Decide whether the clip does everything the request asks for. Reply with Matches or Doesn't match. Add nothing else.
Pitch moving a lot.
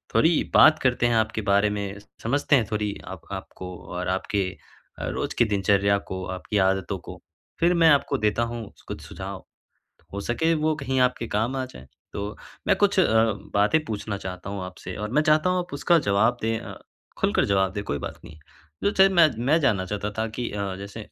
Matches